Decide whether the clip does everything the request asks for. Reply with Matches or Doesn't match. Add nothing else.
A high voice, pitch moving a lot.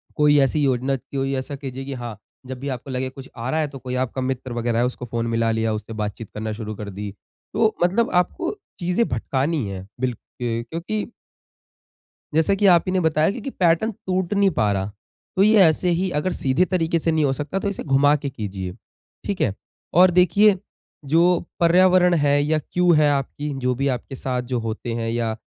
Doesn't match